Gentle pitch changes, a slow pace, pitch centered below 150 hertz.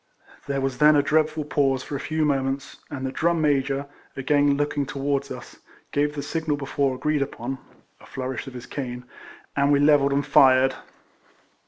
No: narrow, 1.5 semitones; average, 180 wpm; medium, 140 Hz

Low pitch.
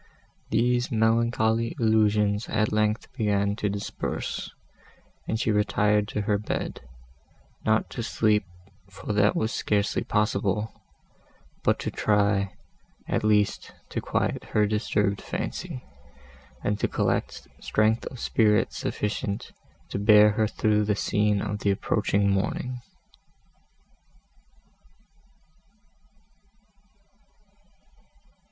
Yes: low, 105 Hz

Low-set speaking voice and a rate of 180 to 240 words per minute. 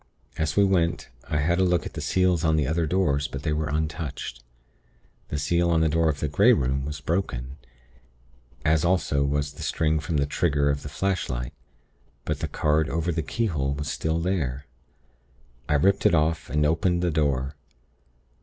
Yes: very low, 75 Hz; average, 185 wpm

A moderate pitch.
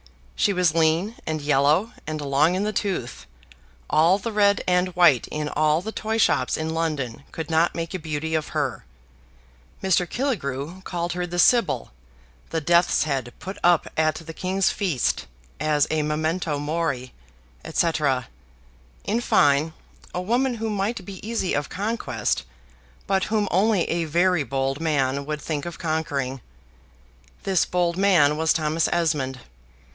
Yes: medium, 165 Hz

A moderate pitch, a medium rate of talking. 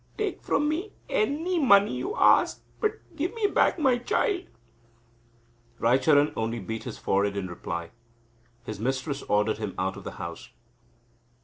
Yes: medium, 145 Hz; average, 145 wpm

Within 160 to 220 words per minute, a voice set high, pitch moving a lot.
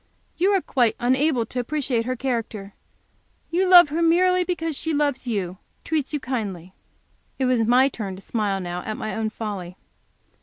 Yes: average, 175 wpm; very high, 250 Hz; wide, 6.2 semitones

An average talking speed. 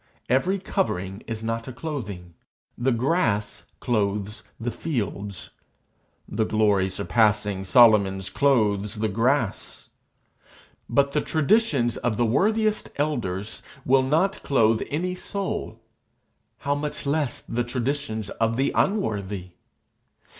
No: slow, 110 wpm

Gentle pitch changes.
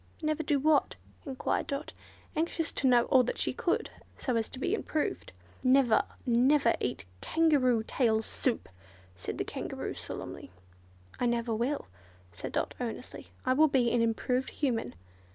No: average, 3.8 semitones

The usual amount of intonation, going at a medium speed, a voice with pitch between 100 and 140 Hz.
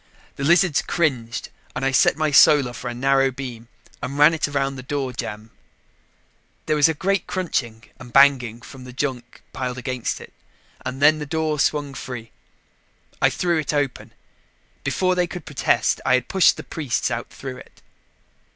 Yes: average, 3.3 semitones; average, 175 wpm; low, 135 Hz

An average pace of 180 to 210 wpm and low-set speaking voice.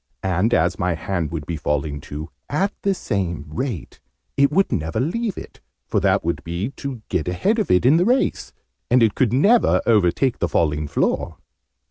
Yes: average, 185 wpm; very low, 95 Hz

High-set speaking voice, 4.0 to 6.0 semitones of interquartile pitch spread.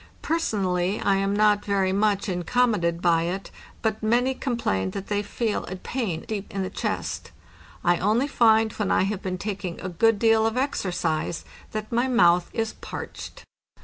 No: high, 205 Hz; average, 3.5 semitones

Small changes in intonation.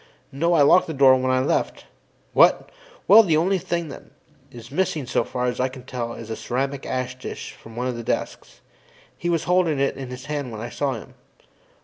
No: average, 4.3 semitones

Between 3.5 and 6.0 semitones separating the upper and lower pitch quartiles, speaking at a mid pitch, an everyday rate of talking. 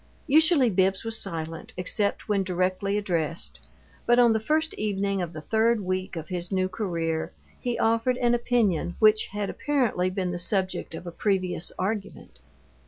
No: average, 3.9 semitones; high, 195 Hz; average, 160 wpm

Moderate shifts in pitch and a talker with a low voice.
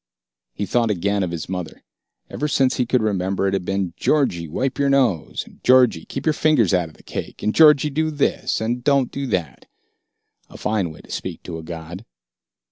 No: wide, 7.3 semitones; low, 105 Hz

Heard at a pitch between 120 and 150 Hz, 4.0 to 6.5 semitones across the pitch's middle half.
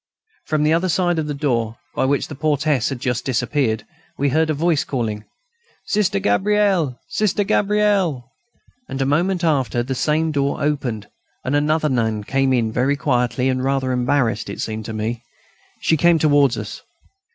Yes: medium, 140 Hz; average, 4.4 semitones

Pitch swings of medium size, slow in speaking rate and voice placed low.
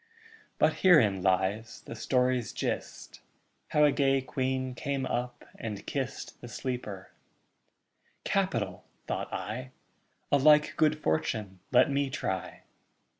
Yes: average, 4.3 semitones; slow, 120 wpm; low, 125 Hz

